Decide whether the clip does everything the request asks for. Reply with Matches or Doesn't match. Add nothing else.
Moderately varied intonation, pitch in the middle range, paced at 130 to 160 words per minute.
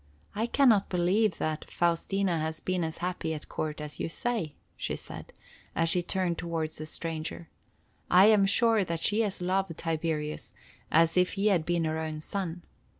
Doesn't match